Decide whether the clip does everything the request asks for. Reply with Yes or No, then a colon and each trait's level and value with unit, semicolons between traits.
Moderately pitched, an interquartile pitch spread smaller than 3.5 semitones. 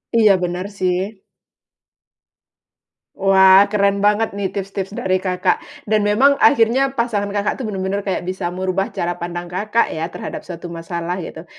No: high, 195 Hz; narrow, 2.5 semitones